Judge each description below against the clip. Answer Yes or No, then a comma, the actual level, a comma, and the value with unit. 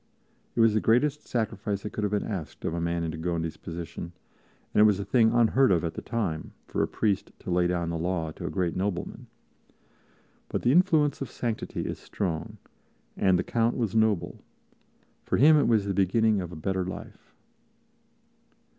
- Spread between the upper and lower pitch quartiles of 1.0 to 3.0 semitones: No, average, 4.7 semitones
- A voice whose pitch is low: Yes, low, 100 Hz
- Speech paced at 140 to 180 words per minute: No, average, 195 wpm